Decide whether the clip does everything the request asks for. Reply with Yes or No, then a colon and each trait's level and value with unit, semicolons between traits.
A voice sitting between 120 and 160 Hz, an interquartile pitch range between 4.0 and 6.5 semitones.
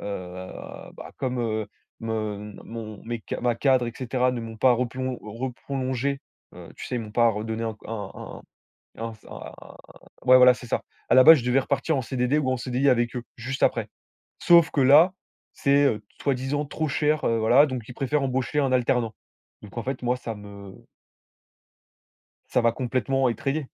No: low, 125 Hz; average, 2.9 semitones